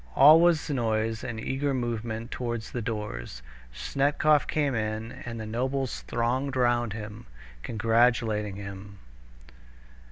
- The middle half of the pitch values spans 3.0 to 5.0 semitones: Yes, average, 3.3 semitones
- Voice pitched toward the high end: No, low, 115 Hz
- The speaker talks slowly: Yes, slow, 120 wpm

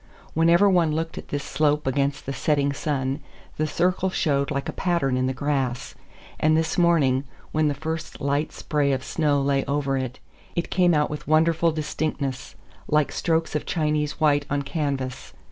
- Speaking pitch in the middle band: Yes, medium, 150 Hz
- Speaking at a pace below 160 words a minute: No, average, 175 wpm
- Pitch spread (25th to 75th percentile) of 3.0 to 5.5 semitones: No, narrow, 2.5 semitones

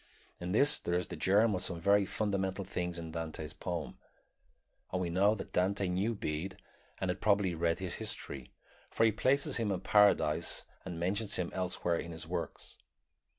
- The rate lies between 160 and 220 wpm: Yes, average, 180 wpm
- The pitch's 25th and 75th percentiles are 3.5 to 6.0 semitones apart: No, average, 3.1 semitones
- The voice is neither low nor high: No, very low, 95 Hz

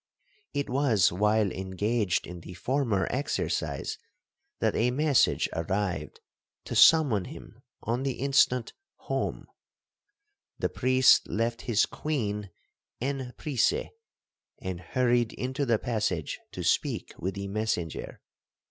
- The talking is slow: Yes, slow, 110 wpm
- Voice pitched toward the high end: No, low, 115 Hz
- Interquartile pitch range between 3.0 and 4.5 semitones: No, average, 5.0 semitones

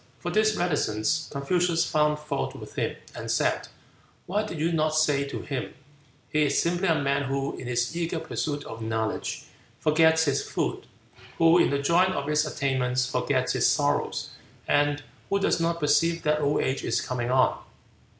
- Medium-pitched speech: Yes, medium, 150 Hz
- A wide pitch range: No, average, 3.3 semitones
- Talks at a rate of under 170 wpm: No, average, 175 wpm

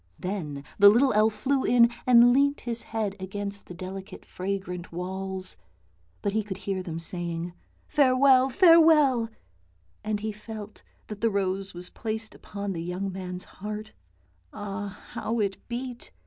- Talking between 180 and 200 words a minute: No, average, 155 wpm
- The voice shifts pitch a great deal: No, average, 3.8 semitones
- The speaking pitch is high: Yes, high, 205 Hz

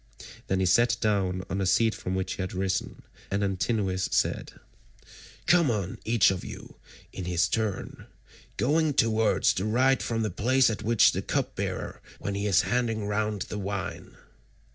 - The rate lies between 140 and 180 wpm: Yes, average, 170 wpm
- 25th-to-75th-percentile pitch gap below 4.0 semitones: Yes, average, 3.3 semitones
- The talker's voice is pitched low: Yes, low, 105 Hz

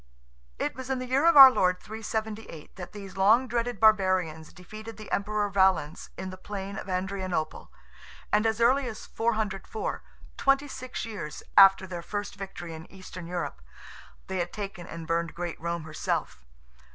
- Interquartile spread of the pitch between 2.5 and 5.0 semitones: Yes, average, 3.9 semitones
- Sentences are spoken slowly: No, average, 155 wpm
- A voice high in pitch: Yes, high, 195 Hz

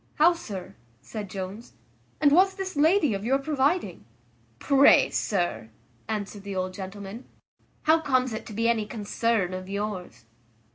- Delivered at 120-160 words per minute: Yes, average, 145 wpm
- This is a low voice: No, high, 220 Hz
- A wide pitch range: Yes, wide, 6.4 semitones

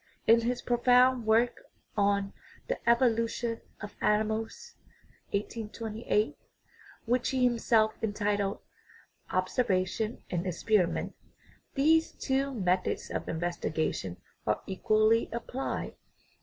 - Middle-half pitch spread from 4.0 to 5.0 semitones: No, average, 3.3 semitones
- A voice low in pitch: No, high, 220 Hz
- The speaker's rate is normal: No, slow, 90 wpm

